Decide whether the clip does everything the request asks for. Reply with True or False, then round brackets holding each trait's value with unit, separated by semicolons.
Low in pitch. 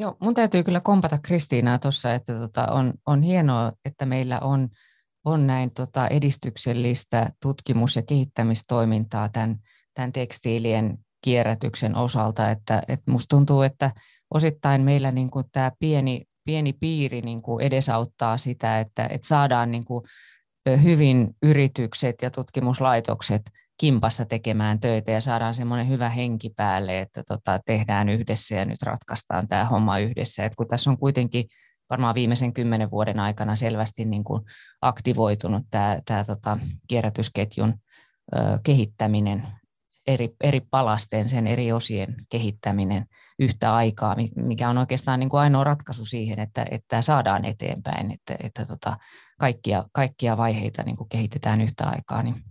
True (120 Hz)